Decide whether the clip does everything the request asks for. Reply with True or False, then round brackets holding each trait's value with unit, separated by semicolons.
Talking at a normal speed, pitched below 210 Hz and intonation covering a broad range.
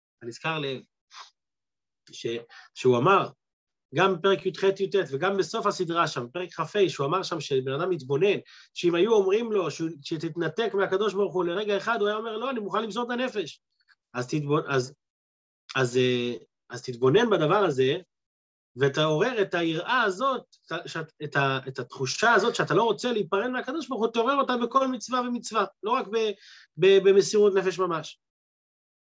False (155 wpm; 185 Hz; 7.2 semitones)